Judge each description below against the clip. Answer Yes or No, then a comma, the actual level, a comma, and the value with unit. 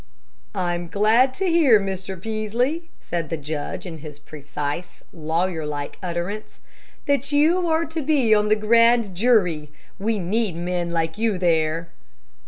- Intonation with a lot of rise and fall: Yes, wide, 5.8 semitones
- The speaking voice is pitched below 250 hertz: Yes, high, 190 Hz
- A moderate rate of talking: Yes, average, 150 wpm